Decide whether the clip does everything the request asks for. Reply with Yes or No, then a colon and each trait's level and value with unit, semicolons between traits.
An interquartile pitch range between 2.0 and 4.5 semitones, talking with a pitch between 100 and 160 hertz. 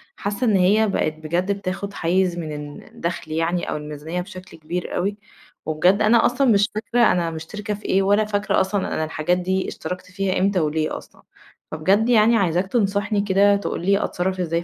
No: average, 3.0 semitones; high, 190 Hz